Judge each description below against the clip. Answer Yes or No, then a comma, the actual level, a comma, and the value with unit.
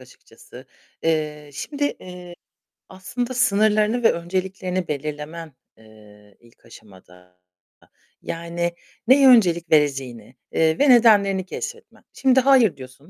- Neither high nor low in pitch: Yes, medium, 170 Hz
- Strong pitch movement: Yes, wide, 7.7 semitones